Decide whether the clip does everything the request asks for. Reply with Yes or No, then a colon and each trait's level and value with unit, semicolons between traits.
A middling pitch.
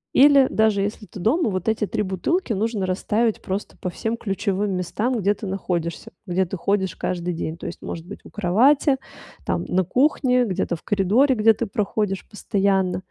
No: high, 200 Hz